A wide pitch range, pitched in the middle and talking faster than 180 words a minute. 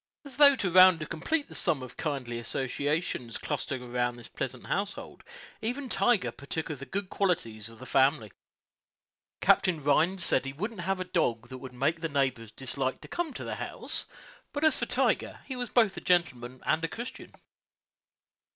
Yes: wide, 7.0 semitones; medium, 155 Hz; average, 190 wpm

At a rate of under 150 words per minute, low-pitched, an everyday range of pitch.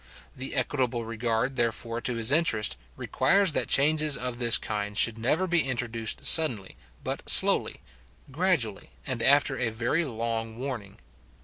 Yes: average, 140 wpm; low, 120 Hz; average, 3.8 semitones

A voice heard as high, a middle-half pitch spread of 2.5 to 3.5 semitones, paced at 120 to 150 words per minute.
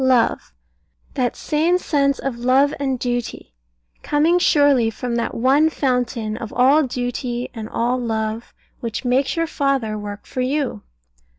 Yes: very high, 250 Hz; average, 3.1 semitones; average, 140 wpm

